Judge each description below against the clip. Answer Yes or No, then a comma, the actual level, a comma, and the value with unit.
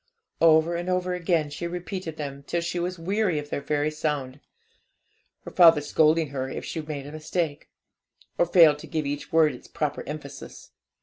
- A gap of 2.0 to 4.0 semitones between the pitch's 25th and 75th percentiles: Yes, average, 2.8 semitones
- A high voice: No, medium, 155 Hz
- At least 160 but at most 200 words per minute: Yes, average, 180 wpm